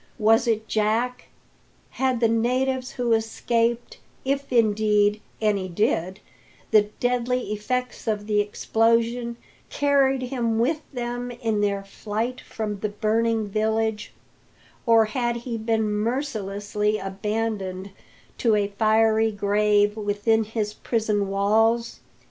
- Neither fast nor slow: No, slow, 115 wpm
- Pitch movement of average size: No, narrow, 2.2 semitones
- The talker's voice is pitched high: Yes, high, 220 Hz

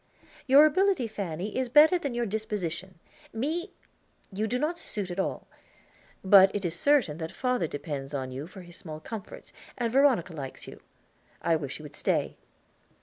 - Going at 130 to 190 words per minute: Yes, average, 170 wpm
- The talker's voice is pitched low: No, high, 200 Hz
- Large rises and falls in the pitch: Yes, wide, 7.8 semitones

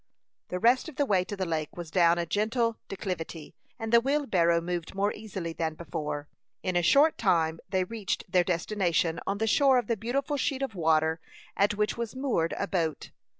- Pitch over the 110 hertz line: Yes, high, 190 Hz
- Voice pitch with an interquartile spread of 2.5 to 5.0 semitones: No, wide, 5.4 semitones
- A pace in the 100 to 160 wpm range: No, average, 195 wpm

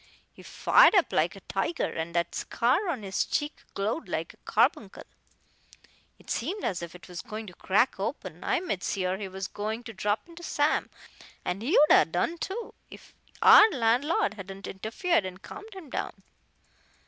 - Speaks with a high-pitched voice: Yes, high, 225 Hz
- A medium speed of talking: Yes, average, 180 wpm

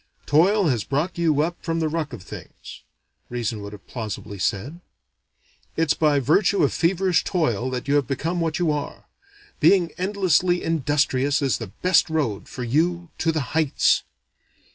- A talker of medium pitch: Yes, medium, 155 Hz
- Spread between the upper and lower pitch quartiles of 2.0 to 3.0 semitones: No, average, 4.9 semitones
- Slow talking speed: No, average, 165 wpm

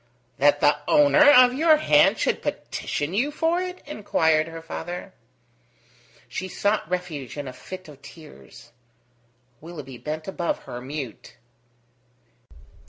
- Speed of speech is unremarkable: No, slow, 125 wpm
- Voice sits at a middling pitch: Yes, medium, 175 Hz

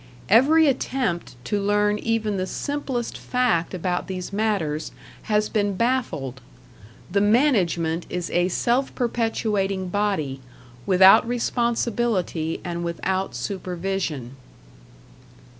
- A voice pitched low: No, high, 200 Hz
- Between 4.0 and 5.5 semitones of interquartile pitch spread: Yes, average, 4.8 semitones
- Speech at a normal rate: No, slow, 100 wpm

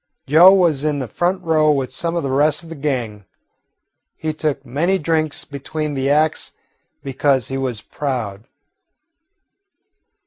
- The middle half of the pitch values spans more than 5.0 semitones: No, average, 3.0 semitones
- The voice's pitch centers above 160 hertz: No, medium, 145 Hz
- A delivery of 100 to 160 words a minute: Yes, average, 145 wpm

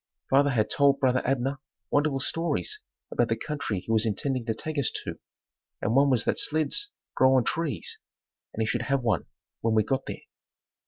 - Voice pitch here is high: No, low, 130 Hz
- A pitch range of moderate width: Yes, average, 3.8 semitones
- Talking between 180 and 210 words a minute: Yes, average, 190 wpm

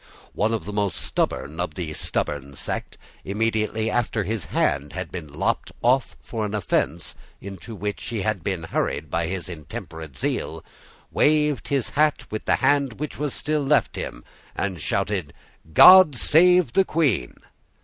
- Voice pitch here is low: Yes, low, 105 Hz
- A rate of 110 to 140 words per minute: No, average, 160 wpm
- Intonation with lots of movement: Yes, wide, 8.3 semitones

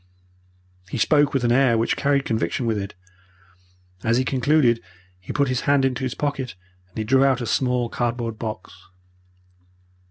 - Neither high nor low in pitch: No, low, 125 Hz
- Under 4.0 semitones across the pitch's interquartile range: Yes, average, 2.9 semitones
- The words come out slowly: No, average, 165 wpm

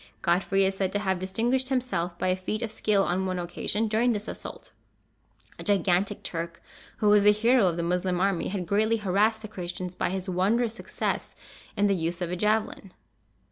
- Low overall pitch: No, high, 195 Hz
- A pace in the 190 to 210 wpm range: Yes, average, 195 wpm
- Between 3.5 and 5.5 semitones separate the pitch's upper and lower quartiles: No, average, 3.1 semitones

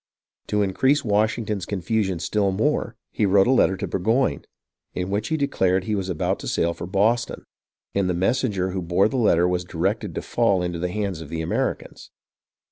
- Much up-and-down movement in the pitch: No, average, 3.4 semitones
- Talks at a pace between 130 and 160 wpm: No, average, 190 wpm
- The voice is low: Yes, low, 100 Hz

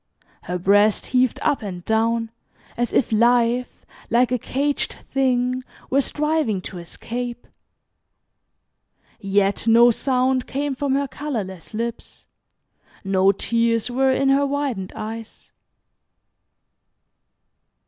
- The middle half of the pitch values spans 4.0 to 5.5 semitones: No, average, 3.6 semitones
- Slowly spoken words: Yes, slow, 105 wpm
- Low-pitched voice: No, high, 240 Hz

